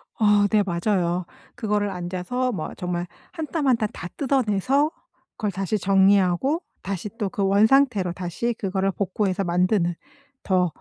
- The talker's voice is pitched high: Yes, high, 200 Hz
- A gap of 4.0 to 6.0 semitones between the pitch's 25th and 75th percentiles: No, average, 3.4 semitones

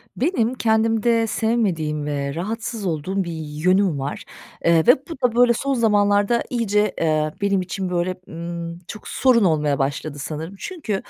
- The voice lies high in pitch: Yes, high, 195 Hz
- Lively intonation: Yes, wide, 6.1 semitones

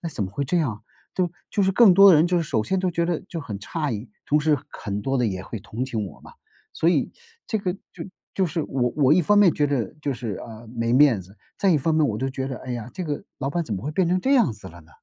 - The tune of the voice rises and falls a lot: Yes, wide, 7.1 semitones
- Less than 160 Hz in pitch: Yes, medium, 140 Hz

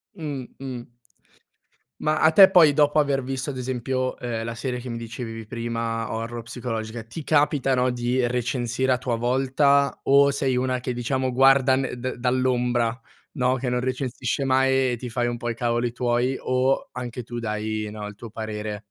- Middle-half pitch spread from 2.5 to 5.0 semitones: No, narrow, 2.1 semitones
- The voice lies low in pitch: Yes, low, 125 Hz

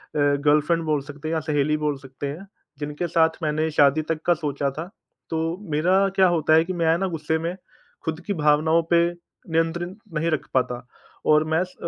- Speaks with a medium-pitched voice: Yes, medium, 155 Hz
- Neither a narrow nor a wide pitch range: No, narrow, 2.1 semitones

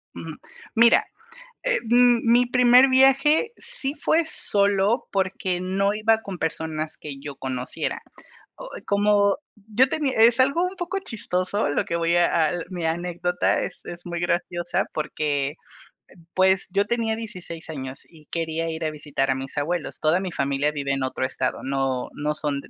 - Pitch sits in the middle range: Yes, medium, 180 Hz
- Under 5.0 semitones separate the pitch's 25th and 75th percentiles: No, wide, 6.9 semitones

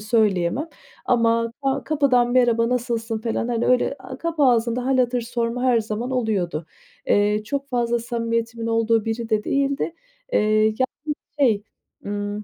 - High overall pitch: Yes, high, 230 Hz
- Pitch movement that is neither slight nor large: No, narrow, 2.1 semitones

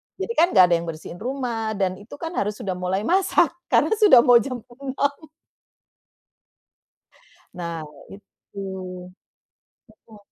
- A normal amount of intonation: No, wide, 6.4 semitones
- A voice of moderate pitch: No, high, 225 Hz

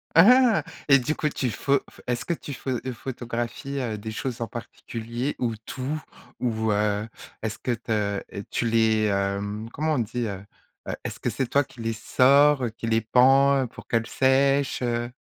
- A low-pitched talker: Yes, low, 120 Hz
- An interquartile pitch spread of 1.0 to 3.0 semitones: No, average, 3.6 semitones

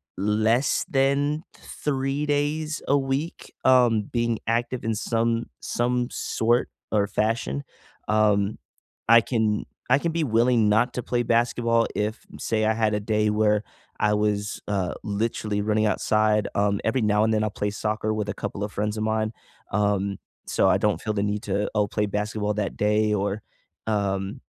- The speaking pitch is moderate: No, low, 110 Hz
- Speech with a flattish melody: Yes, narrow, 2.1 semitones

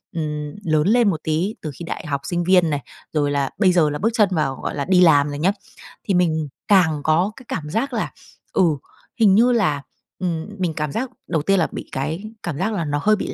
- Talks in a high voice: No, medium, 165 Hz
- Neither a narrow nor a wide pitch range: Yes, average, 4.3 semitones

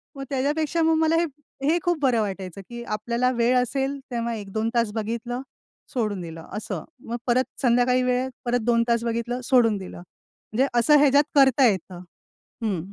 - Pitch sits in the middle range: No, high, 240 Hz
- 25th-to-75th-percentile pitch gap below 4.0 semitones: Yes, average, 3.3 semitones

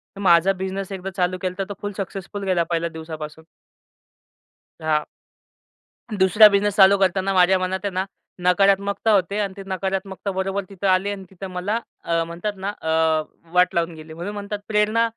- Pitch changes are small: Yes, narrow, 1.9 semitones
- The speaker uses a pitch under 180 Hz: No, high, 190 Hz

